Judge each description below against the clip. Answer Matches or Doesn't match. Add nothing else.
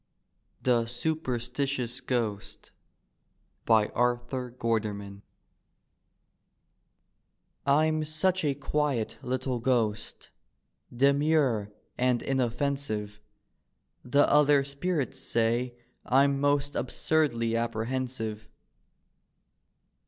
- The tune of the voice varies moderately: Matches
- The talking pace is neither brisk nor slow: Doesn't match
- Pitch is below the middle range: Matches